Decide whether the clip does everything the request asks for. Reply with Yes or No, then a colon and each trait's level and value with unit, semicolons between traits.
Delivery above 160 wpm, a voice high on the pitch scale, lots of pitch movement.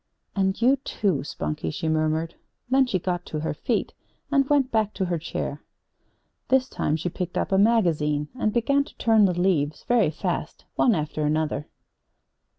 No: average, 170 wpm; medium, 180 Hz; wide, 7.0 semitones